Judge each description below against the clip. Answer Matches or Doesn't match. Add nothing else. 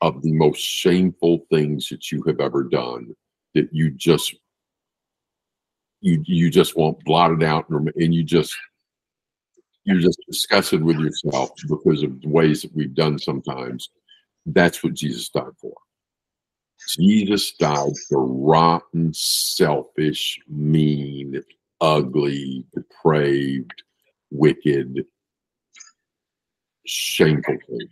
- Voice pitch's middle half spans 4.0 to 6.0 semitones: Doesn't match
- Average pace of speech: Doesn't match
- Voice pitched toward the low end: Matches